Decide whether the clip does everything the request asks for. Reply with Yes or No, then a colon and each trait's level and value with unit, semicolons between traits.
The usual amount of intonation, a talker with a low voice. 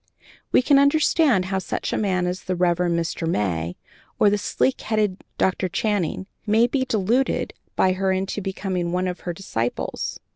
No: average, 3.2 semitones; high, 190 Hz